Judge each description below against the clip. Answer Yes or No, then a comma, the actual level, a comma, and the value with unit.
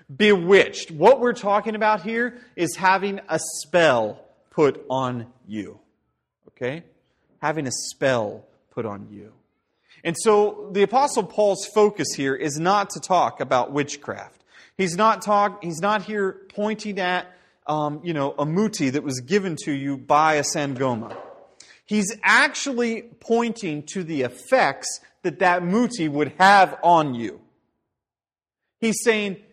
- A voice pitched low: No, medium, 180 Hz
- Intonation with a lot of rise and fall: Yes, wide, 6.0 semitones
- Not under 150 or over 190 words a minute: No, average, 140 wpm